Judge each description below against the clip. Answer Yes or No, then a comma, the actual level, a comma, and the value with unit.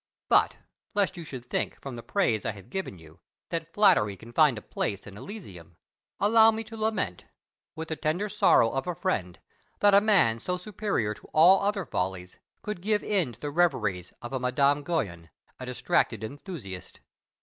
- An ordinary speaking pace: Yes, average, 180 wpm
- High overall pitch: No, medium, 145 Hz